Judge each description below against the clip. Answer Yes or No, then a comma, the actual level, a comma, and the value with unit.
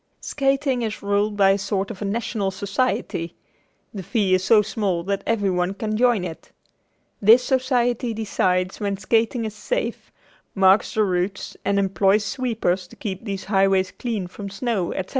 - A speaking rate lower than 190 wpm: Yes, average, 160 wpm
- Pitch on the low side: No, high, 205 Hz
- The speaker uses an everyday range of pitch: Yes, average, 3.0 semitones